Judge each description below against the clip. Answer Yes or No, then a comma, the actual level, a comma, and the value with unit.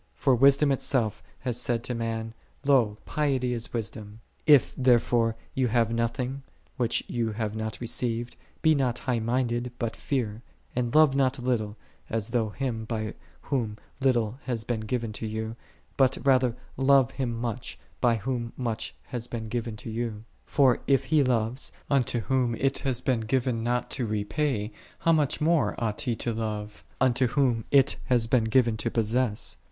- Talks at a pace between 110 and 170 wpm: No, average, 180 wpm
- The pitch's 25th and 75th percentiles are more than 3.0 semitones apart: No, average, 2.7 semitones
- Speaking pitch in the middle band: No, low, 120 Hz